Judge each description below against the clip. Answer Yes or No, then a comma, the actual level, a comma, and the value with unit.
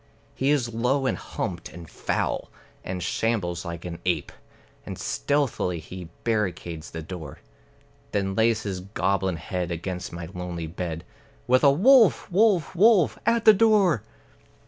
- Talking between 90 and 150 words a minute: Yes, average, 145 wpm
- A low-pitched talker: Yes, very low, 95 Hz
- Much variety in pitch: Yes, wide, 8.3 semitones